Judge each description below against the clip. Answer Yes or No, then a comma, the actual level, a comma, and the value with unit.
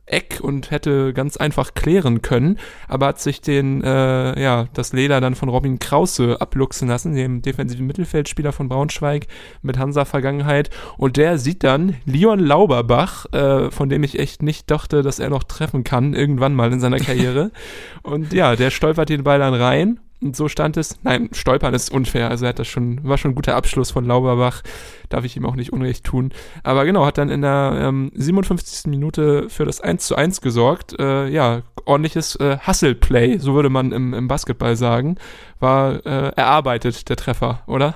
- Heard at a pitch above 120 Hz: Yes, low, 135 Hz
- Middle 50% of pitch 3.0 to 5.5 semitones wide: No, narrow, 2.6 semitones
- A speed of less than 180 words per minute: No, fast, 190 wpm